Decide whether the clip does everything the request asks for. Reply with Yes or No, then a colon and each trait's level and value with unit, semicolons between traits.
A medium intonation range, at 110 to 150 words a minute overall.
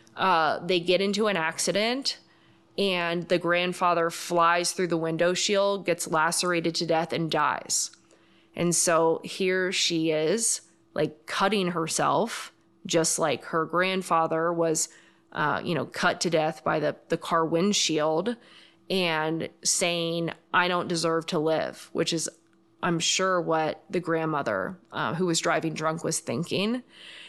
No: narrow, 1.9 semitones; average, 145 wpm